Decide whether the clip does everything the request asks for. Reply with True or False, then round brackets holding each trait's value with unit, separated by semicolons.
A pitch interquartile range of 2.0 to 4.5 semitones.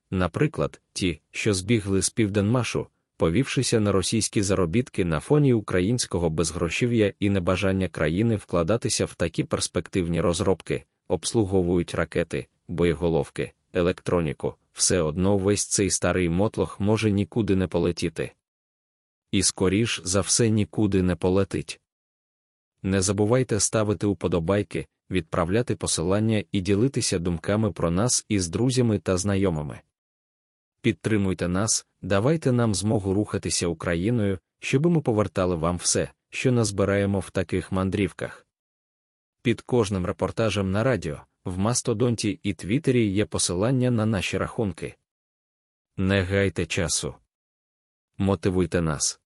True (3.5 semitones)